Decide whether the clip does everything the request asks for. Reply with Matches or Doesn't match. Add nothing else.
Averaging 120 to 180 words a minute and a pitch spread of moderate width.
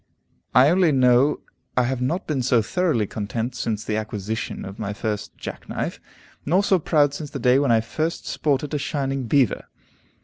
Matches